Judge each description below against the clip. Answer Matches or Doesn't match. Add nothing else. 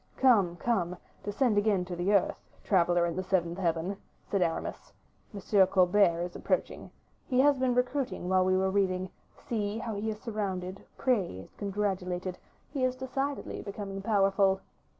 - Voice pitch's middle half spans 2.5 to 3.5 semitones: Matches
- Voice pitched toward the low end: Doesn't match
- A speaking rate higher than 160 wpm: Doesn't match